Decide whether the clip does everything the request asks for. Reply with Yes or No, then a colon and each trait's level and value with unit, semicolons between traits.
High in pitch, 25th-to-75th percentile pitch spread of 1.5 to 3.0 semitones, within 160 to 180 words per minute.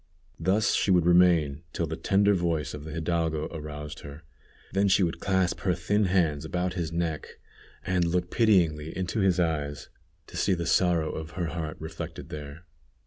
No: very low, 85 Hz; average, 2.7 semitones; average, 175 wpm